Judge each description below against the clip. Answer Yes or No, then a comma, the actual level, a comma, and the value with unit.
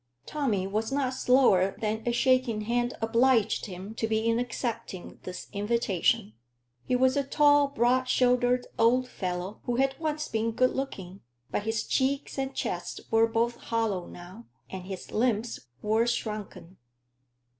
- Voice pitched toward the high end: Yes, high, 230 Hz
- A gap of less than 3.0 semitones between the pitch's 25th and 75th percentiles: No, average, 3.4 semitones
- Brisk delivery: No, average, 150 wpm